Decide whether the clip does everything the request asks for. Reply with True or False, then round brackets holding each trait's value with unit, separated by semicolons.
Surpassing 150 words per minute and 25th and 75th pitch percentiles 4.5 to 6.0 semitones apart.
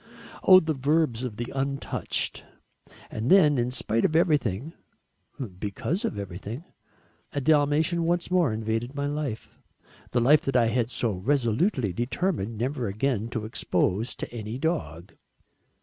False (140 wpm; 5.2 semitones)